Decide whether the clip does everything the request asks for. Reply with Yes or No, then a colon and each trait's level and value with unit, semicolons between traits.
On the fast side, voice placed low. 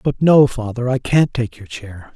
Yes: fast, 220 wpm; low, 125 Hz